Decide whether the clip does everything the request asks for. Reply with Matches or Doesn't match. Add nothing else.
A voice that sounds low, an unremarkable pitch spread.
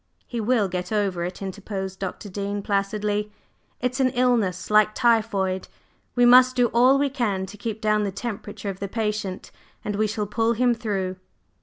Doesn't match